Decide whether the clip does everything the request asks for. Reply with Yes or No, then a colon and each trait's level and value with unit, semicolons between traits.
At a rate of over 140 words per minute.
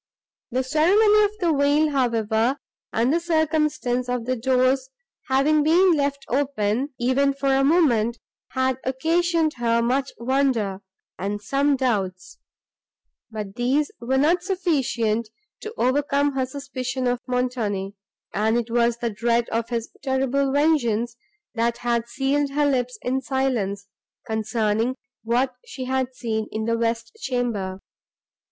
No: slow, 135 wpm